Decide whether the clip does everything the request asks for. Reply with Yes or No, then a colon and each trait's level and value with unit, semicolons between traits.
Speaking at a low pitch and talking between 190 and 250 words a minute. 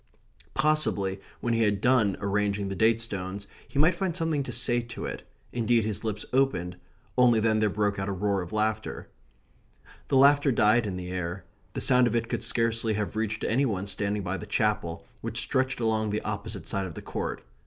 Yes: low, 110 Hz; average, 200 wpm